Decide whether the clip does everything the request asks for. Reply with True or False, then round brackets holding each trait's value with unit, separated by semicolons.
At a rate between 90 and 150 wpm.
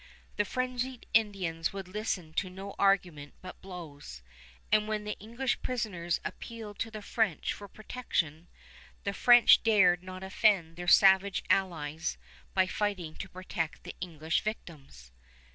True (140 wpm)